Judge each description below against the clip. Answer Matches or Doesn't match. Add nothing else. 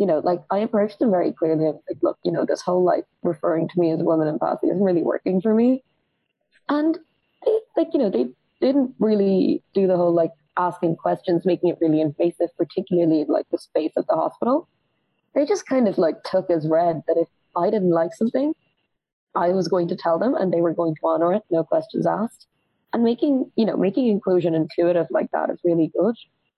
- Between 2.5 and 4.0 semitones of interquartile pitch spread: Doesn't match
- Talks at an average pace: Doesn't match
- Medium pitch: Matches